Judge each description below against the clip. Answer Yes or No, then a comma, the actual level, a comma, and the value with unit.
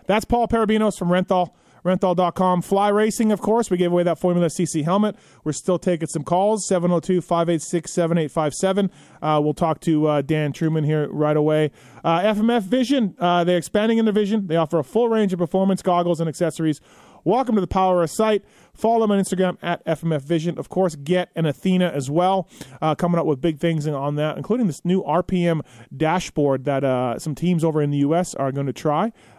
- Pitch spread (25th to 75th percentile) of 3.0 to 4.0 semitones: Yes, average, 3.6 semitones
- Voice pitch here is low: No, medium, 175 Hz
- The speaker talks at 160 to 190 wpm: No, average, 200 wpm